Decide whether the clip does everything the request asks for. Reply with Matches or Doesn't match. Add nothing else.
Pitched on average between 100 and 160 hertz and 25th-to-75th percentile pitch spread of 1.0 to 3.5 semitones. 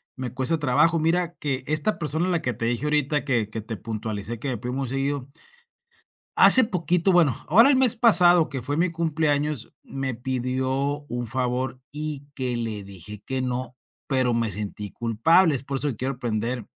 Doesn't match